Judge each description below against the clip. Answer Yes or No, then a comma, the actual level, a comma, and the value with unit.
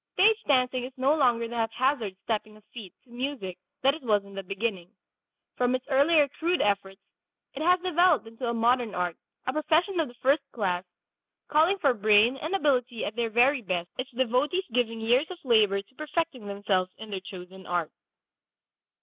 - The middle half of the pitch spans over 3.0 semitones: Yes, wide, 5.6 semitones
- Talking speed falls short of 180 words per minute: No, average, 185 wpm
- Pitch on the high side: Yes, high, 245 Hz